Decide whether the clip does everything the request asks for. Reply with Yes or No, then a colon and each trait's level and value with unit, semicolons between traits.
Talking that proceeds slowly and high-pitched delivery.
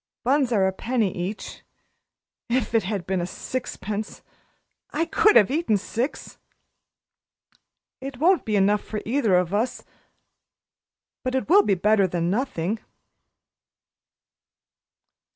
Yes: slow, 115 wpm; high, 220 Hz